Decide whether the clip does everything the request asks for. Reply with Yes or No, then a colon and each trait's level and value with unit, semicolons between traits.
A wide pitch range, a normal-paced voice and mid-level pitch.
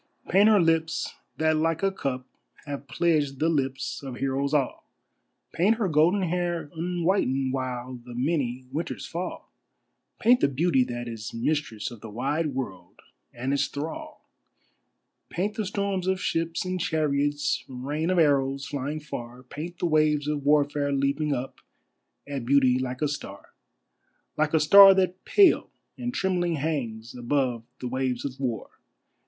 No: average, 4.4 semitones; average, 150 wpm; medium, 145 Hz